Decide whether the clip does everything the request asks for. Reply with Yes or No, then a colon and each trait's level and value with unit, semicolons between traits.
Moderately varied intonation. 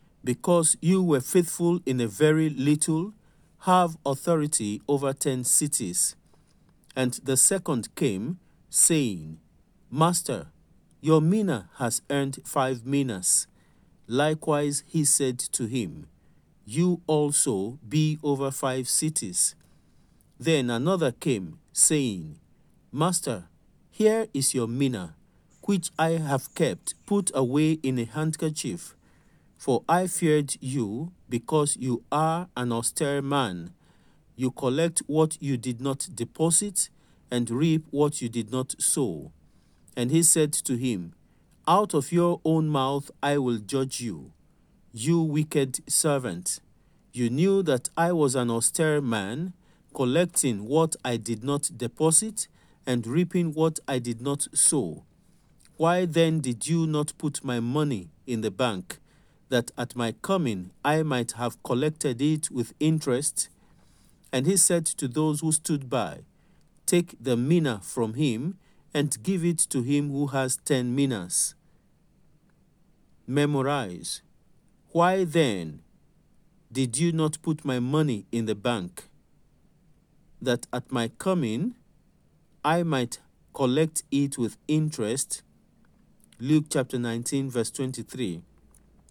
Yes: average, 4.5 semitones